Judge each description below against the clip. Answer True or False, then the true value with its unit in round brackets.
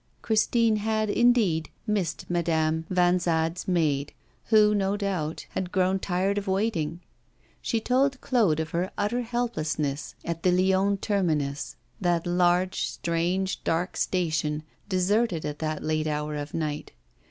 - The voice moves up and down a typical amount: True (4.4 semitones)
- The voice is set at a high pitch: False (180 Hz)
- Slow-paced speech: True (130 wpm)